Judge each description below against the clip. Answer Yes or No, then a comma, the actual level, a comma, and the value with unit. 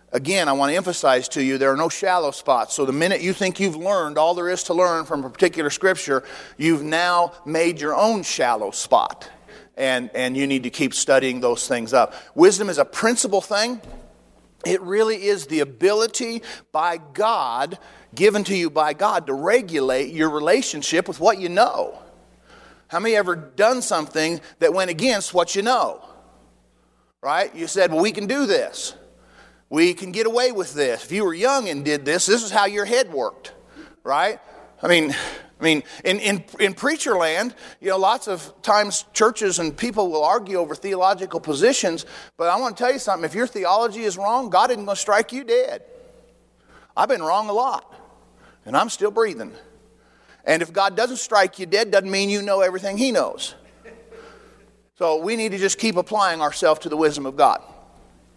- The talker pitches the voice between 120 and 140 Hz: No, high, 190 Hz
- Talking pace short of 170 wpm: No, average, 190 wpm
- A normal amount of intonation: No, wide, 5.9 semitones